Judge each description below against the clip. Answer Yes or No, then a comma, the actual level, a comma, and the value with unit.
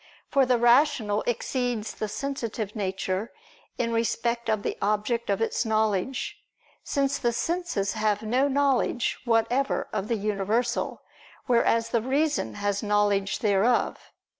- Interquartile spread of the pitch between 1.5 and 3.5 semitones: Yes, average, 3.2 semitones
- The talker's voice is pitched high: Yes, high, 230 Hz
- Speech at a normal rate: No, slow, 130 wpm